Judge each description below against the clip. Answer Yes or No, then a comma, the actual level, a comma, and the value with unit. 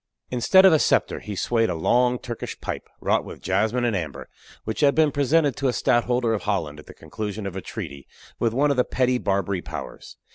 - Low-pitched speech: Yes, low, 120 Hz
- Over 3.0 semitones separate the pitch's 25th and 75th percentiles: Yes, average, 4.5 semitones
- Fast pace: Yes, fast, 215 wpm